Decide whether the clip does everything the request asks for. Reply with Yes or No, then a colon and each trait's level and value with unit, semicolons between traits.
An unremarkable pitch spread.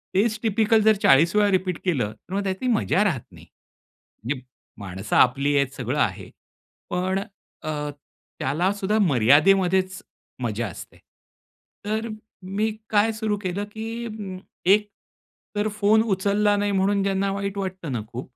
No: wide, 6.3 semitones